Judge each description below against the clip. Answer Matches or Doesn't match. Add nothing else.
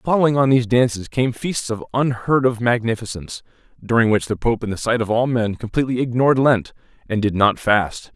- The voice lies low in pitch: Matches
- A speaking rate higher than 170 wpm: Matches